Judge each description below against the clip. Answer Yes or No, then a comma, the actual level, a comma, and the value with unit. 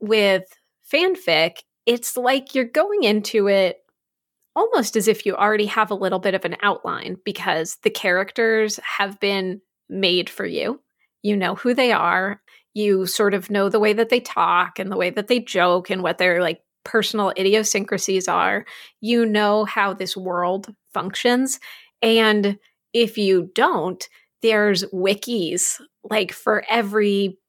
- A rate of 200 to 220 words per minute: No, average, 155 wpm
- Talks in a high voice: Yes, high, 205 Hz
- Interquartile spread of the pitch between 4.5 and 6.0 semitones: No, average, 3.0 semitones